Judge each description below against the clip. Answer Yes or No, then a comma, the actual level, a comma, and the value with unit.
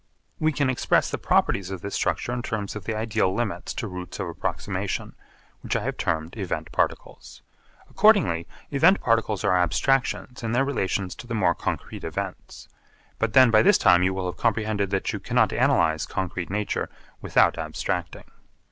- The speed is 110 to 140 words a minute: No, average, 175 wpm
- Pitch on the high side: No, low, 105 Hz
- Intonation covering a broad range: No, average, 4.5 semitones